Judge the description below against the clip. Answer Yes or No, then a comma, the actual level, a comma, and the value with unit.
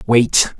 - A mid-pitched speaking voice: No, low, 115 Hz